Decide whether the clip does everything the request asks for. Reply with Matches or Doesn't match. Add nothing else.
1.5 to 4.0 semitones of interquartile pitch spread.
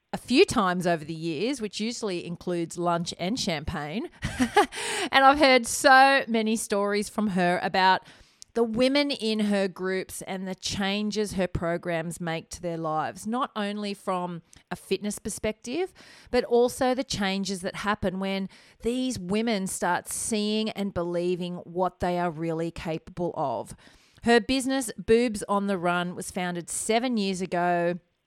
Doesn't match